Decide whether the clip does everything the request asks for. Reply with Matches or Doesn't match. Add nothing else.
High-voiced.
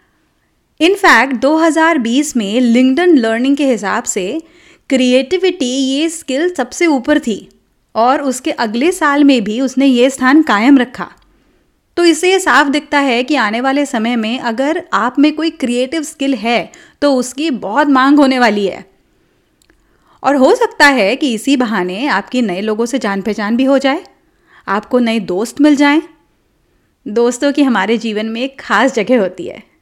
Matches